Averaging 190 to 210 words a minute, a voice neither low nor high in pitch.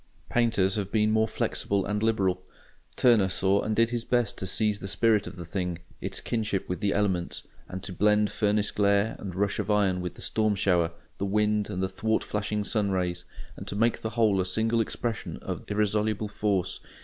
No: average, 200 wpm; low, 105 Hz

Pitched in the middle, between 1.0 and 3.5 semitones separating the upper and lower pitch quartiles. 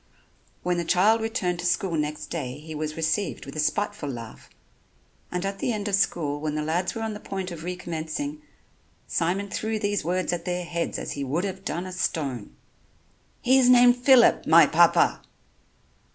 No: medium, 180 Hz; average, 4.7 semitones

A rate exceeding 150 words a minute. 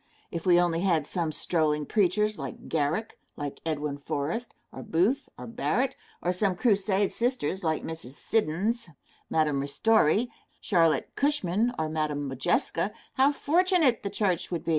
No: average, 145 wpm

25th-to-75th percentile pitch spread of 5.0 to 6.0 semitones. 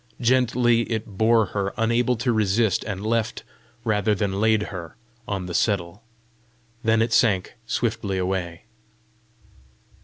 No: average, 3.1 semitones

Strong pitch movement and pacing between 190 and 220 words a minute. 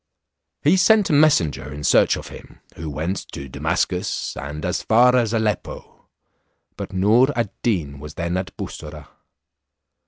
No: wide, 8.0 semitones; average, 150 wpm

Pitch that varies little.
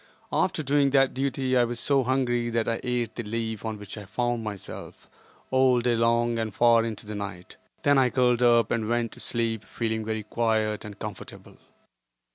Yes: narrow, 2.0 semitones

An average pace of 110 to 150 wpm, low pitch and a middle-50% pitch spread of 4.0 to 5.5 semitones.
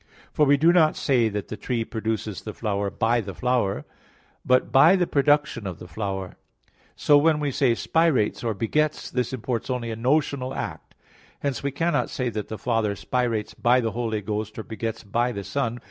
No: average, 190 wpm; low, 120 Hz; average, 4.4 semitones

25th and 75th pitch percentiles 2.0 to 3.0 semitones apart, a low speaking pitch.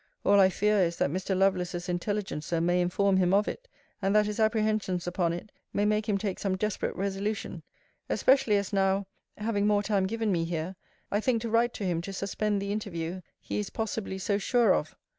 No: narrow, 2.5 semitones; high, 200 Hz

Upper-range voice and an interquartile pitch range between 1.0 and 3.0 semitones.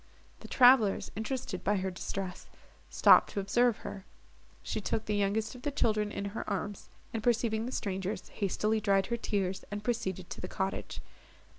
Yes: high, 210 Hz; narrow, 2.5 semitones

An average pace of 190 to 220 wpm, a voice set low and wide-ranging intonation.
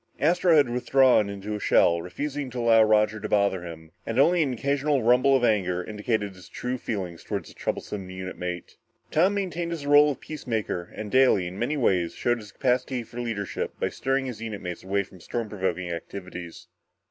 Yes: average, 195 wpm; low, 110 Hz; wide, 5.9 semitones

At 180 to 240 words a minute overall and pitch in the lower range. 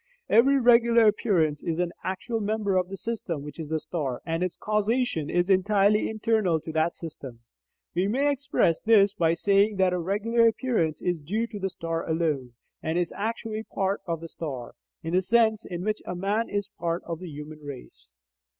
No: average, 190 wpm; medium, 185 Hz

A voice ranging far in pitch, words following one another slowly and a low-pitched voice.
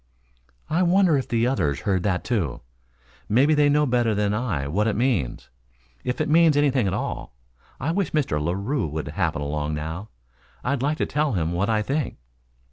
No: wide, 8.8 semitones; average, 185 wpm; low, 115 Hz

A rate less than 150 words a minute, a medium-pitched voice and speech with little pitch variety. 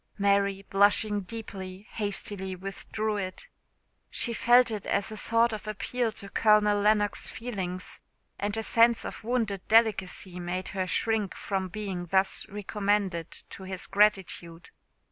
No: slow, 135 wpm; high, 205 Hz; narrow, 2.3 semitones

